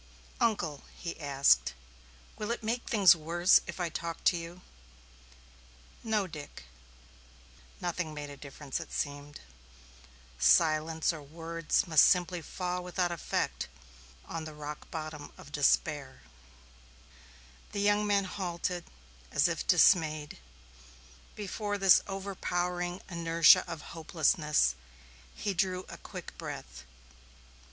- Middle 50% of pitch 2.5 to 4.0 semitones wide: Yes, average, 3.3 semitones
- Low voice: No, medium, 170 Hz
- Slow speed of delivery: Yes, slow, 115 wpm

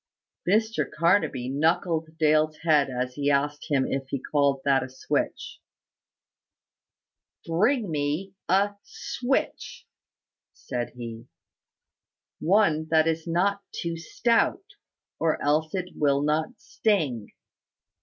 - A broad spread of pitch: No, average, 4.5 semitones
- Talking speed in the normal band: No, slow, 110 wpm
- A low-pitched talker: No, medium, 155 Hz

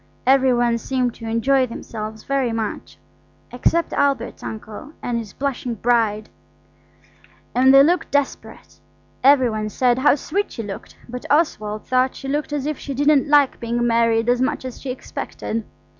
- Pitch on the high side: Yes, very high, 250 Hz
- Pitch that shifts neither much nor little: Yes, average, 3.2 semitones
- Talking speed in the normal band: Yes, average, 160 wpm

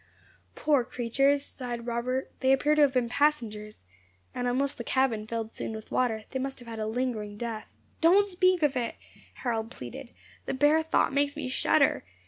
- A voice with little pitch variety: No, average, 3.7 semitones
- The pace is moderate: Yes, average, 180 wpm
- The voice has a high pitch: Yes, very high, 255 Hz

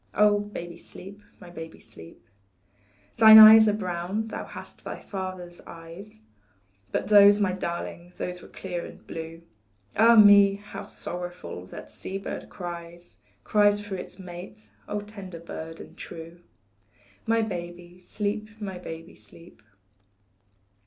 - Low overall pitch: No, medium, 185 Hz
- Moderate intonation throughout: Yes, average, 3.2 semitones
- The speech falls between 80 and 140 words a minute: Yes, slow, 135 wpm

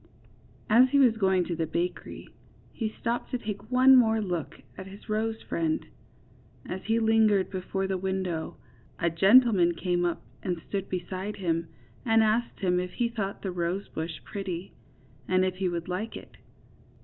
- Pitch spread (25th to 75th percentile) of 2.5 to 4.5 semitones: Yes, average, 3.8 semitones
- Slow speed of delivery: No, average, 165 wpm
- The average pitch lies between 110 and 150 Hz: No, high, 190 Hz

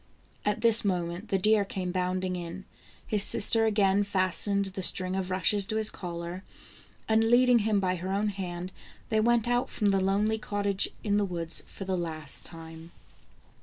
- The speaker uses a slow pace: No, average, 175 wpm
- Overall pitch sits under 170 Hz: No, high, 195 Hz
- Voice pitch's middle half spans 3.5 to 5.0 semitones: No, narrow, 2.6 semitones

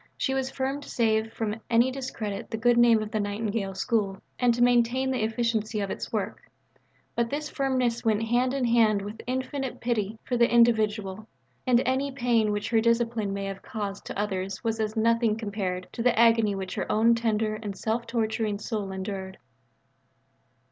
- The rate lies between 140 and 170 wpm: No, average, 180 wpm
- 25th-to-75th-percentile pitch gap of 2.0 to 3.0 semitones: Yes, narrow, 2.4 semitones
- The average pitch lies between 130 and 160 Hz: No, high, 225 Hz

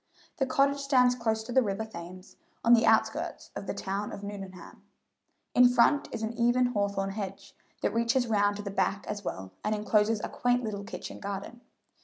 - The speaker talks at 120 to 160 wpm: No, average, 190 wpm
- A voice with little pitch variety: No, average, 3.3 semitones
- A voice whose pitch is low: No, high, 220 Hz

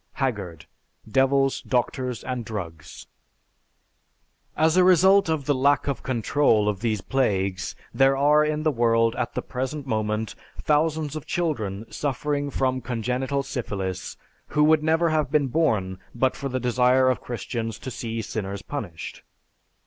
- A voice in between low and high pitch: No, low, 130 Hz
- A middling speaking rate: Yes, average, 145 wpm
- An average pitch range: Yes, average, 4.7 semitones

